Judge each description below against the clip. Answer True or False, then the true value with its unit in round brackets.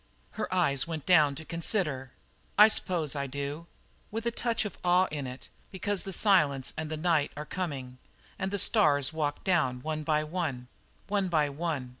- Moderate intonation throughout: True (4.7 semitones)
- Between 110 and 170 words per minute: False (180 wpm)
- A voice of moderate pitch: True (155 Hz)